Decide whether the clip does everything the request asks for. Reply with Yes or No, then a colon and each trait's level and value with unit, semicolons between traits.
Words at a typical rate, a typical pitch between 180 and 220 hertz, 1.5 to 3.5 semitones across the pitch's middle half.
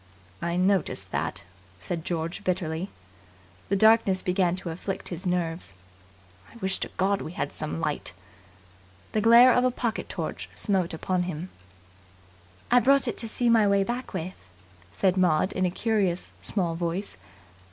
No: average, 155 wpm; medium, 185 Hz; average, 4.1 semitones